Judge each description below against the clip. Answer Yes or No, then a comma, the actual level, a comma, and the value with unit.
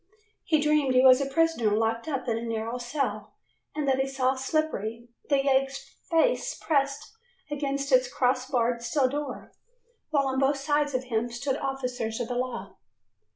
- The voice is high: Yes, very high, 265 Hz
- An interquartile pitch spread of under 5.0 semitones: Yes, narrow, 2.5 semitones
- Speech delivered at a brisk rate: No, average, 170 wpm